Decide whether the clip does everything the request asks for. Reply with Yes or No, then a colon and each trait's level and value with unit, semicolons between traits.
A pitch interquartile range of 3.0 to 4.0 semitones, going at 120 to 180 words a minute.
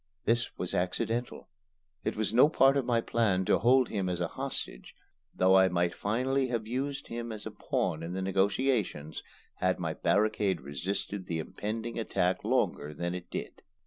No: average, 4.7 semitones; average, 175 wpm